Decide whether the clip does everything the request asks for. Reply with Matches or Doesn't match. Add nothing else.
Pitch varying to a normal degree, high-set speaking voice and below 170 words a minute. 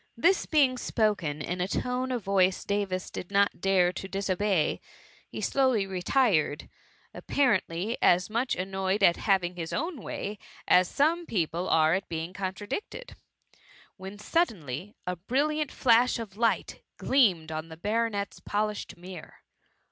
Matches